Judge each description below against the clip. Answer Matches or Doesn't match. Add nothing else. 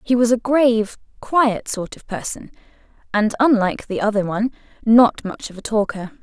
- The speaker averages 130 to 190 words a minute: Matches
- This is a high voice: Matches